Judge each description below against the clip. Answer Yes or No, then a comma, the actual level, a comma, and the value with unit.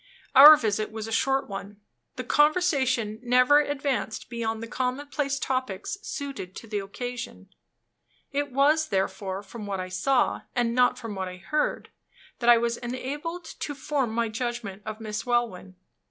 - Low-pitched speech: No, high, 240 Hz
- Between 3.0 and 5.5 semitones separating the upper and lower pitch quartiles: Yes, average, 4.4 semitones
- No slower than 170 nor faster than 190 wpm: No, average, 155 wpm